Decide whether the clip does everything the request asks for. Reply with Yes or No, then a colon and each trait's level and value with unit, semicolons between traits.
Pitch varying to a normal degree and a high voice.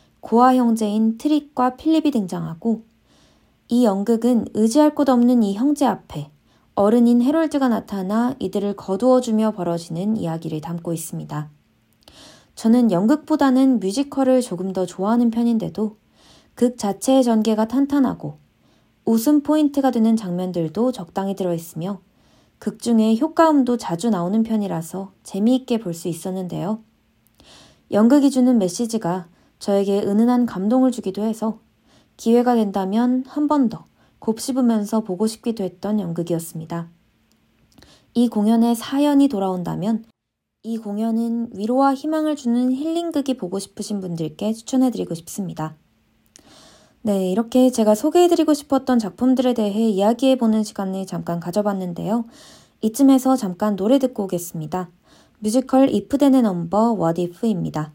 Yes: average, 4.8 semitones; high, 220 Hz